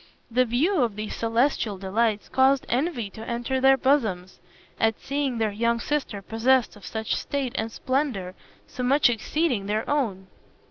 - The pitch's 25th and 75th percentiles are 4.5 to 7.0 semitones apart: No, average, 3.8 semitones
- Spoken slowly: No, average, 155 wpm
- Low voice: No, high, 235 Hz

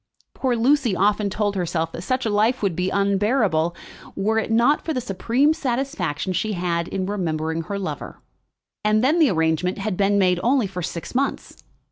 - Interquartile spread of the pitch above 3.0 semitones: Yes, average, 4.9 semitones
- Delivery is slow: No, average, 180 wpm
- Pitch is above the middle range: Yes, high, 200 Hz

